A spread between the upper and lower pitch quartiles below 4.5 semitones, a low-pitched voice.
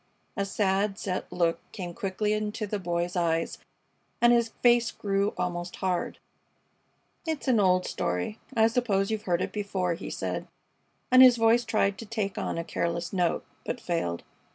No: average, 4.0 semitones; high, 195 Hz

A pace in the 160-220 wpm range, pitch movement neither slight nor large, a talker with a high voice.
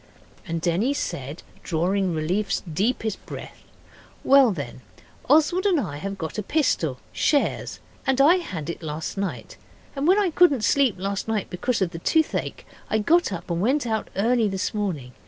No: average, 170 wpm; wide, 8.3 semitones; high, 205 Hz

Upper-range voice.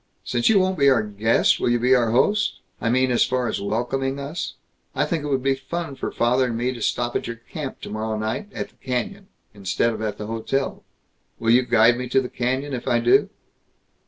No: low, 125 Hz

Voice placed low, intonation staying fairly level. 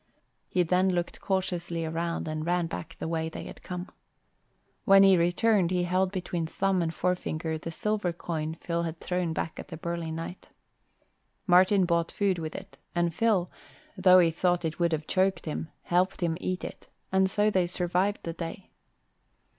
No: medium, 175 Hz; narrow, 2.0 semitones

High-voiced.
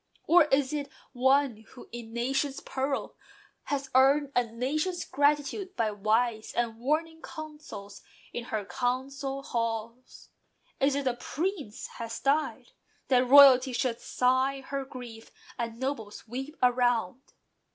Yes: very high, 260 Hz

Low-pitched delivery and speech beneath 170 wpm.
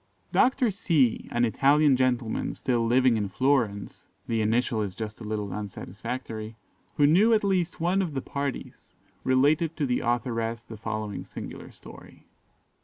Yes: low, 125 Hz; average, 150 wpm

